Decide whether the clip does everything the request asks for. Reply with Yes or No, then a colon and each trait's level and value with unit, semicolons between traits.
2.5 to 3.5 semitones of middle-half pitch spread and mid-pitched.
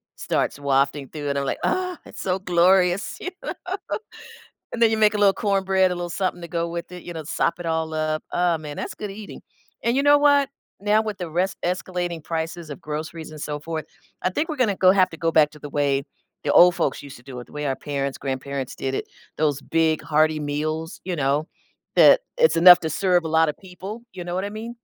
No: average, 4.1 semitones; medium, 170 Hz